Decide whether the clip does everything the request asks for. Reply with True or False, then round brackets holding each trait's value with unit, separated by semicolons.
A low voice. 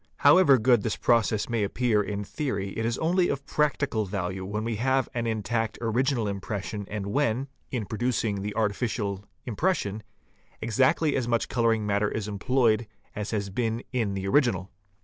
True (110 Hz)